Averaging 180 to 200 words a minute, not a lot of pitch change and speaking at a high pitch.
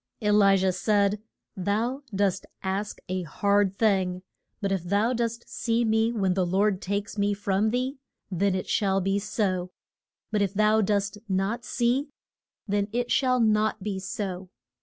No: average, 160 wpm; narrow, 2.3 semitones; high, 205 Hz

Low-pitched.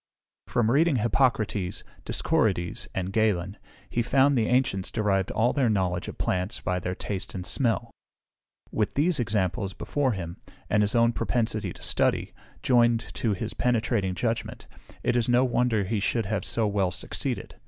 Yes: low, 110 Hz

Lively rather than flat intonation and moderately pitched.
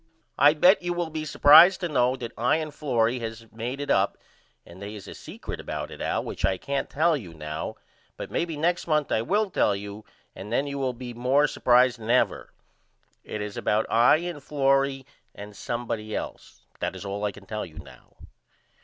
No: wide, 5.7 semitones; low, 125 Hz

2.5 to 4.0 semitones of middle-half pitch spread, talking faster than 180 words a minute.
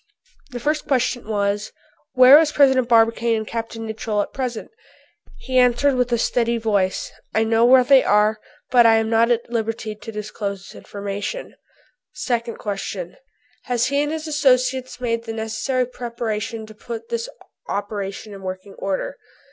No: average, 3.0 semitones; average, 160 wpm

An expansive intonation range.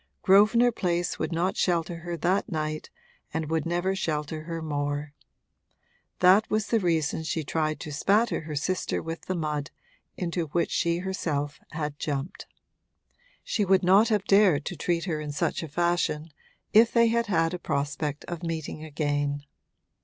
No: average, 3.5 semitones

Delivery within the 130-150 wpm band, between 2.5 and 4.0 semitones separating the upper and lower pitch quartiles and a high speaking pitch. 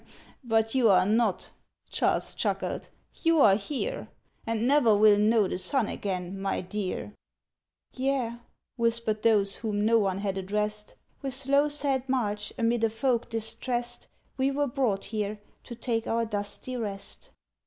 Yes: average, 145 wpm; average, 3.6 semitones; high, 225 Hz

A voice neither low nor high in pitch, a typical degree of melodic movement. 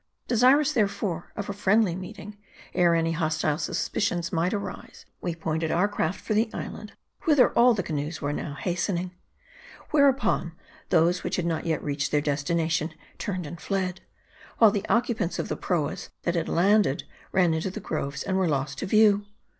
Yes: medium, 180 Hz; average, 4.3 semitones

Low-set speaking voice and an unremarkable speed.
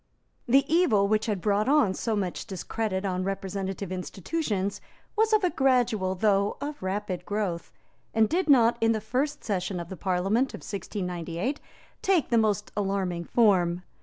No: high, 205 Hz; average, 155 wpm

